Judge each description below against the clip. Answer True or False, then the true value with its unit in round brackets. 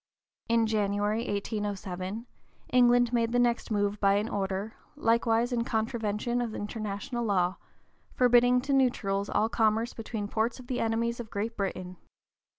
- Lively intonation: False (2.7 semitones)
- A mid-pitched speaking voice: False (225 Hz)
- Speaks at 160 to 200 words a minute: False (145 wpm)